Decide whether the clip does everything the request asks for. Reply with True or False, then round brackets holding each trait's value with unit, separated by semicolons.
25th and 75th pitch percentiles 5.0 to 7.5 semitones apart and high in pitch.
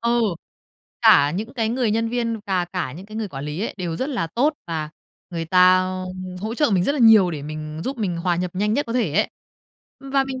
True (5.6 semitones; 200 Hz)